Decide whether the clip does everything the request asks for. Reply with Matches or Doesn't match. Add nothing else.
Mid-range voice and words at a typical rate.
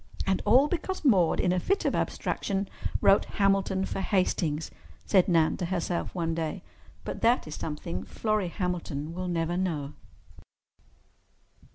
Matches